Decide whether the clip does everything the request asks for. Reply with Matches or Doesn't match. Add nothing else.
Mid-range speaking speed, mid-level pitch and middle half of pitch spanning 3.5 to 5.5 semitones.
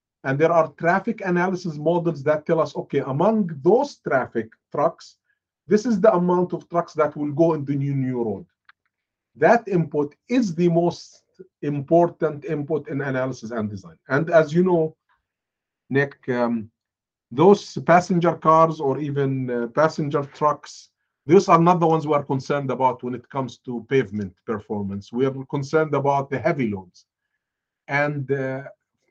Matches